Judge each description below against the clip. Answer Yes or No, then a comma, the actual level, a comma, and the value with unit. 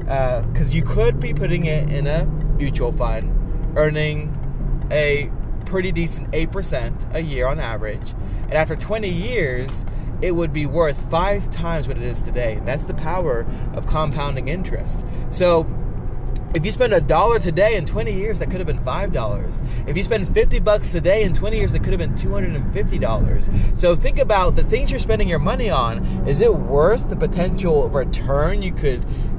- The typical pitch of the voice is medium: Yes, medium, 150 Hz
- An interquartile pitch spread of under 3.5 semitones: No, average, 4.0 semitones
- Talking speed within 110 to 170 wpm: No, average, 190 wpm